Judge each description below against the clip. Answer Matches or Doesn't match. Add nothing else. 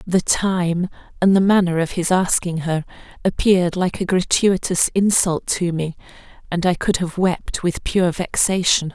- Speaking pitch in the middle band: Matches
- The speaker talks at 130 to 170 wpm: Matches